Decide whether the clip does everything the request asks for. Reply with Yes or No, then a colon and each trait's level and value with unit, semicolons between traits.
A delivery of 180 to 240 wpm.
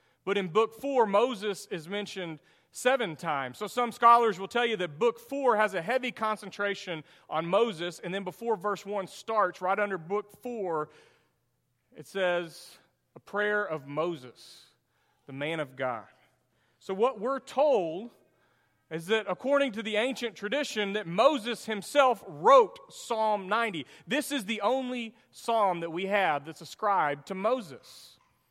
No: average, 155 wpm